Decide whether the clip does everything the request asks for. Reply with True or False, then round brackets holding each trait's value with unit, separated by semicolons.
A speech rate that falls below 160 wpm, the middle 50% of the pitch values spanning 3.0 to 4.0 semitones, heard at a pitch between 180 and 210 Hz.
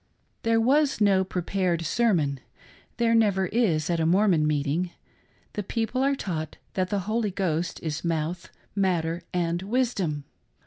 False (150 wpm; 5.0 semitones; 185 Hz)